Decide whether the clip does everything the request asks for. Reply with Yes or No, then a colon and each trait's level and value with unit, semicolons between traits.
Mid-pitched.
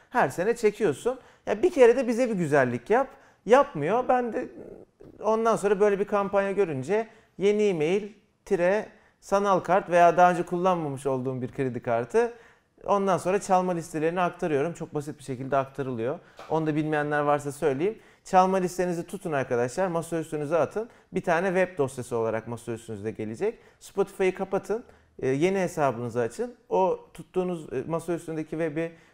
Yes: medium, 180 Hz